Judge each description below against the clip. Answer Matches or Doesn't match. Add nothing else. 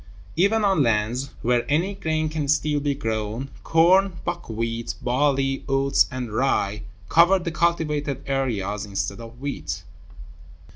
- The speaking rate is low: Matches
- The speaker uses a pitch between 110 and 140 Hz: Matches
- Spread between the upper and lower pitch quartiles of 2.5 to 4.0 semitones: Doesn't match